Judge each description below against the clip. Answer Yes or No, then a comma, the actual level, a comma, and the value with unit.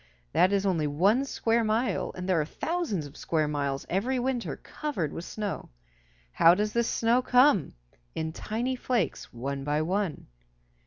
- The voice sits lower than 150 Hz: No, high, 195 Hz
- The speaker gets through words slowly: No, average, 160 wpm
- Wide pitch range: Yes, wide, 7.2 semitones